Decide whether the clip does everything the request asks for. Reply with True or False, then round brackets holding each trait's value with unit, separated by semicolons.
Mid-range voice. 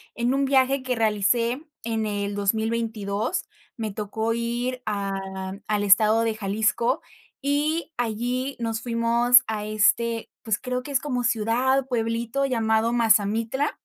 False (230 Hz)